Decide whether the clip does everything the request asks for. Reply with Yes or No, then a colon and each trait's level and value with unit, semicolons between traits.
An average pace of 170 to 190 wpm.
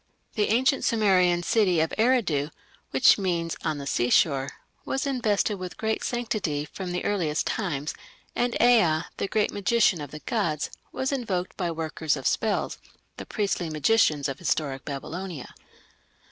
No: average, 145 wpm